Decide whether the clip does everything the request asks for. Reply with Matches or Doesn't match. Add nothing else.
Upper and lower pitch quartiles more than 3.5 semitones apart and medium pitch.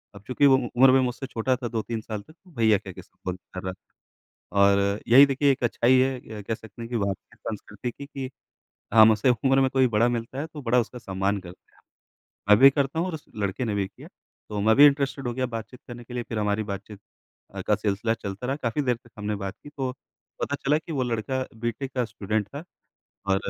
Doesn't match